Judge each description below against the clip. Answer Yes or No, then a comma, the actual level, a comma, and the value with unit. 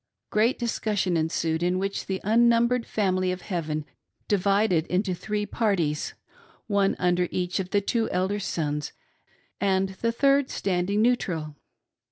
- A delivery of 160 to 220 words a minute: No, average, 140 wpm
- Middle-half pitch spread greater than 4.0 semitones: No, average, 3.3 semitones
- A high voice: Yes, high, 195 Hz